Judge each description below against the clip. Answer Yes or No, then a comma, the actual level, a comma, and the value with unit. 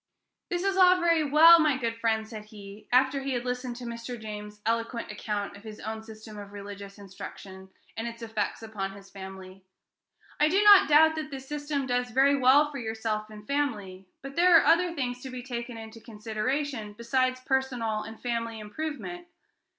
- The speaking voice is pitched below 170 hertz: No, high, 235 Hz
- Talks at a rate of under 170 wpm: No, average, 185 wpm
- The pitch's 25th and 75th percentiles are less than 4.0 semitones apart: No, average, 4.6 semitones